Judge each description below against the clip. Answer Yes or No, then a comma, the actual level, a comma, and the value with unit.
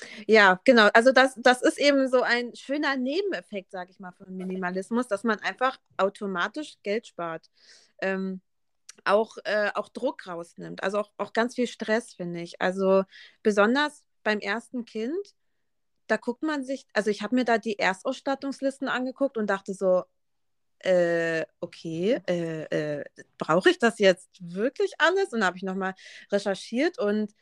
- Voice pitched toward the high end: Yes, high, 215 Hz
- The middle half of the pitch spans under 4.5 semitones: No, average, 5.1 semitones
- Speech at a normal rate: Yes, average, 160 wpm